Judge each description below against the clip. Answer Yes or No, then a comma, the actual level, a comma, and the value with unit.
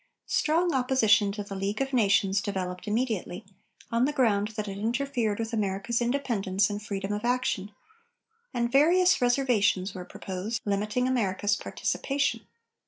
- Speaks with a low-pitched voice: No, high, 215 Hz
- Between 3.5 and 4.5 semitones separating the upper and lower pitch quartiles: Yes, average, 4.0 semitones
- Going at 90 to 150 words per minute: Yes, average, 140 wpm